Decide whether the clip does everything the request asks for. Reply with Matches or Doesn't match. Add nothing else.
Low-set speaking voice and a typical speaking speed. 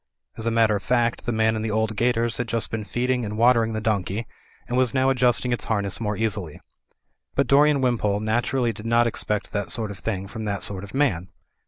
Doesn't match